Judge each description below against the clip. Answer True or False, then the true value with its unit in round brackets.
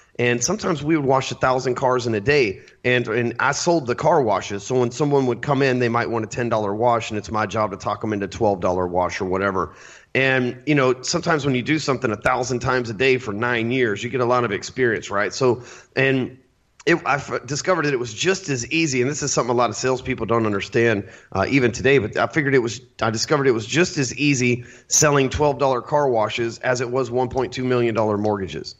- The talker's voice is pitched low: True (125 Hz)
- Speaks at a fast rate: True (250 wpm)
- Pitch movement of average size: True (3.1 semitones)